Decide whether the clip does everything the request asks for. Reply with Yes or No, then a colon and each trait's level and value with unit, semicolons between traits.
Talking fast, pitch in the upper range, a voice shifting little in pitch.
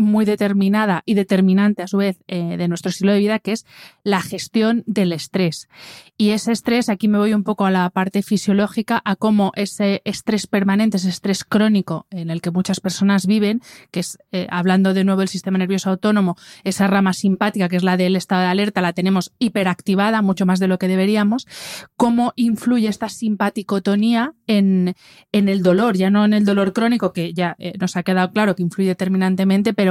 Yes: fast, 200 wpm; high, 195 Hz; narrow, 2.2 semitones